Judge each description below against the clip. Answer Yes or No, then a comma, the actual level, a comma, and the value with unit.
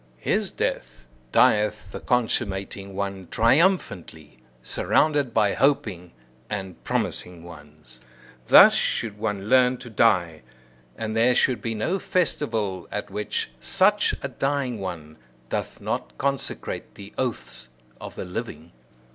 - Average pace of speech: No, slow, 120 wpm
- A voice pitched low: Yes, low, 105 Hz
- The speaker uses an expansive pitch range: Yes, wide, 5.9 semitones